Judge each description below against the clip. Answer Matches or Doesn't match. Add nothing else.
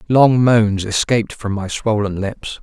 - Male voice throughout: Matches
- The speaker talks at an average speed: Matches